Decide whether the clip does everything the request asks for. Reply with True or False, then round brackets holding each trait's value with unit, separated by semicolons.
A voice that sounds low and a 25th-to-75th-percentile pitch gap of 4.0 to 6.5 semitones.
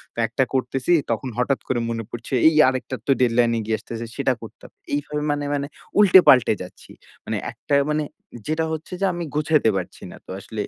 True (130 Hz; 4.3 semitones)